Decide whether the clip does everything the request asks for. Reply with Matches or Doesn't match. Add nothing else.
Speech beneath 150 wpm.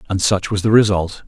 Doesn't match